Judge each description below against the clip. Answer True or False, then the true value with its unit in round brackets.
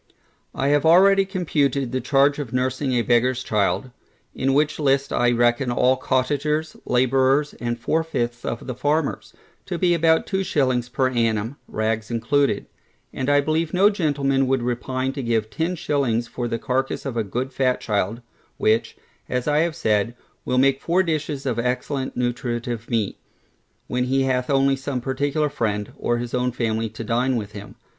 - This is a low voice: True (130 Hz)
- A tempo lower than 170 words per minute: False (175 wpm)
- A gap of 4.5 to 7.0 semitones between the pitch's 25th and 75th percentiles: False (3.2 semitones)